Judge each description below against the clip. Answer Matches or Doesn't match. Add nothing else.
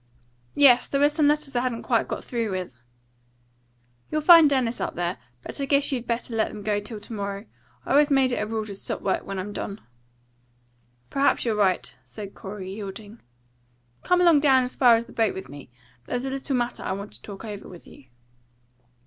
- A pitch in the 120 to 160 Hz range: Doesn't match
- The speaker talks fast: Matches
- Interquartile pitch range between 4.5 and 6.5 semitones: Matches